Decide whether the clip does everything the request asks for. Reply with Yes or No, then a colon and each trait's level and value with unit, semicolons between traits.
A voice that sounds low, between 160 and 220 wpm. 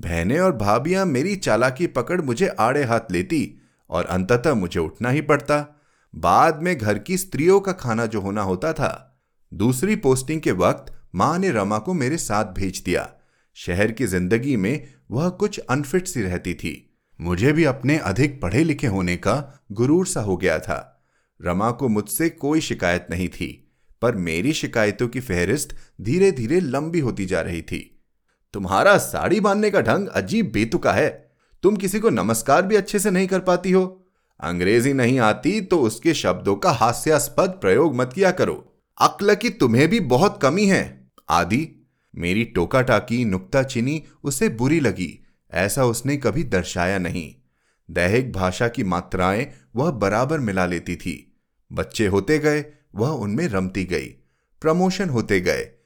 Yes: low, 125 Hz; average, 165 wpm